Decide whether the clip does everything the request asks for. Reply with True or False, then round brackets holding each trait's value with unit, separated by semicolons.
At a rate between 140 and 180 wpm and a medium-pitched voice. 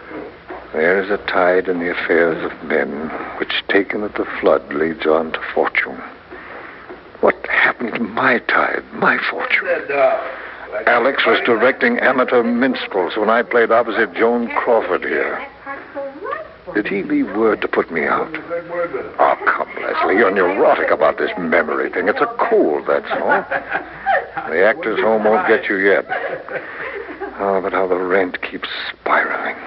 False (150 wpm; 275 Hz)